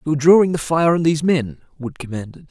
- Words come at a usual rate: No, fast, 215 wpm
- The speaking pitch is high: No, medium, 150 Hz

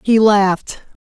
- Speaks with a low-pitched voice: No, high, 205 Hz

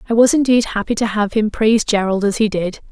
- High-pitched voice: Yes, high, 215 Hz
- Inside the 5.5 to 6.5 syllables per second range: Yes, 6.0 syllables/s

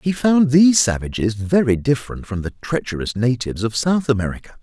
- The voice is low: Yes, low, 125 Hz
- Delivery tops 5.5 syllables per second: Yes, 5.8 syllables/s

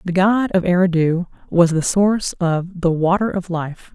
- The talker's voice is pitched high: No, medium, 180 Hz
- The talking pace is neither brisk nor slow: Yes, average, 180 wpm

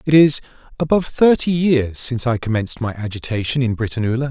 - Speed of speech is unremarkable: Yes, average, 165 wpm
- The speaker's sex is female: No, male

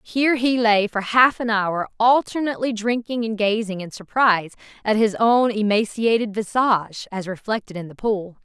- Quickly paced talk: No, average, 165 wpm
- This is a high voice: Yes, high, 215 Hz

